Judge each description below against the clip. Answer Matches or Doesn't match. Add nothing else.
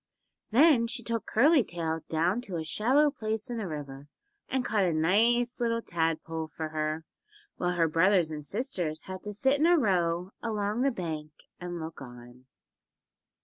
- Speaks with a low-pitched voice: Doesn't match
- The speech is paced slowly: Doesn't match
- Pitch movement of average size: Doesn't match